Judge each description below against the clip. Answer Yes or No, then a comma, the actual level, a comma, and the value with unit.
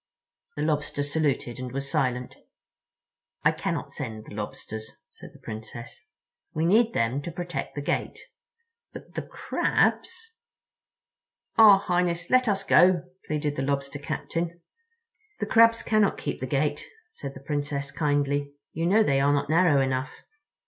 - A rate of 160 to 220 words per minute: No, average, 145 wpm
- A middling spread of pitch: Yes, average, 4.3 semitones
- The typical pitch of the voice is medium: Yes, medium, 145 Hz